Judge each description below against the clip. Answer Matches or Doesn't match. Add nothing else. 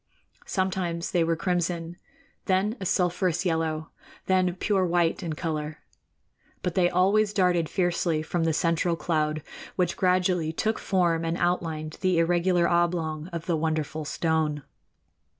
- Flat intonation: Matches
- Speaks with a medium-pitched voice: Matches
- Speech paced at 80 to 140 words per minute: Matches